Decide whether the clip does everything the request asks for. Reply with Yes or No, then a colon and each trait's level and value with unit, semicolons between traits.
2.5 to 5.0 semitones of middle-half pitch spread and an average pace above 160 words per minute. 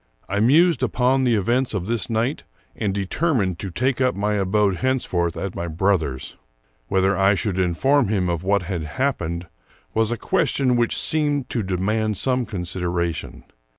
No: wide, 5.5 semitones; average, 170 wpm